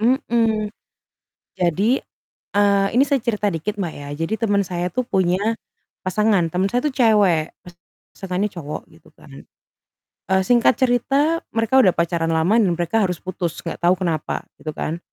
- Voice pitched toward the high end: Yes, high, 195 Hz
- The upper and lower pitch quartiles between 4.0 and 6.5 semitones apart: Yes, average, 4.7 semitones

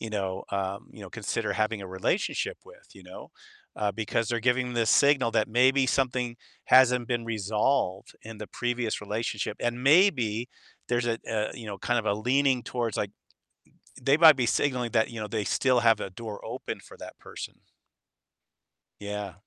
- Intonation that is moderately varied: Yes, average, 3.1 semitones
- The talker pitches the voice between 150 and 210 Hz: No, low, 115 Hz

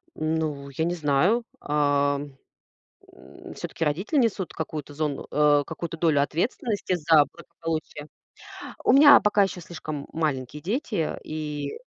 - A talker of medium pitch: Yes, medium, 155 Hz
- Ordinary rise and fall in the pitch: Yes, average, 3.2 semitones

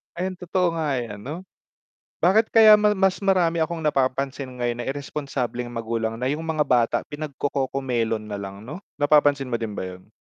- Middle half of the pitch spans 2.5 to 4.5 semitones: No, wide, 5.5 semitones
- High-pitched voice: No, medium, 140 Hz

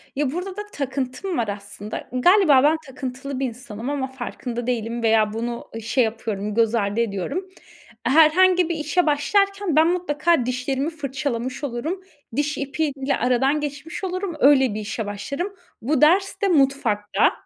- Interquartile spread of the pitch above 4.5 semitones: Yes, average, 5.1 semitones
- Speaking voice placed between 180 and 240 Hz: No, very high, 270 Hz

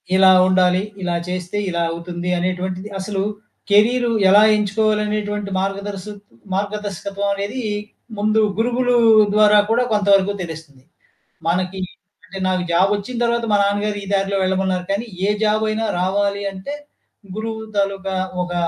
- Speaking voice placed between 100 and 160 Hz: No, high, 200 Hz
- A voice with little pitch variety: Yes, narrow, 2.2 semitones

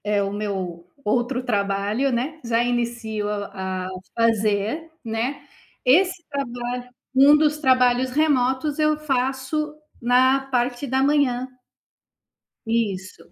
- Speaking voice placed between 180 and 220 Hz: No, high, 245 Hz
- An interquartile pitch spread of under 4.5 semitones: Yes, average, 4.0 semitones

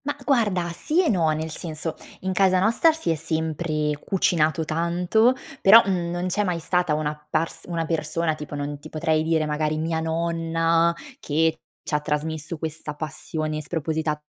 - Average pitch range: No, narrow, 2.2 semitones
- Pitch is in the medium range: Yes, medium, 160 Hz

